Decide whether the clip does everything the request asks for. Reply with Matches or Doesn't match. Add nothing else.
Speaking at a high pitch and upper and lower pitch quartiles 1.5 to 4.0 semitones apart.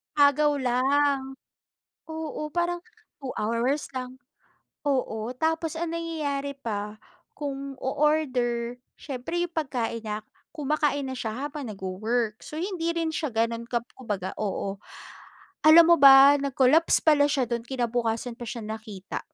Doesn't match